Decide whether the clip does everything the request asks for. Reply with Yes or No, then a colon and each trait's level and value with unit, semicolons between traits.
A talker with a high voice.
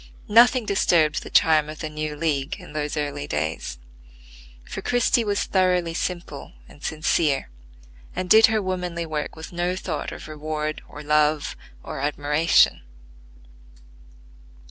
No: medium, 155 Hz